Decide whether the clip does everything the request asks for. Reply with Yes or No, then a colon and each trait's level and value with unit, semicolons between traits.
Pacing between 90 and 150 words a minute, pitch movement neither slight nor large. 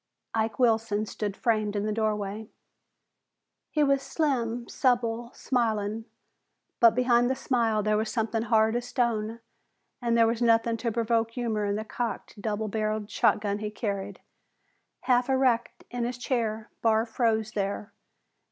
No: average, 145 wpm; narrow, 2.0 semitones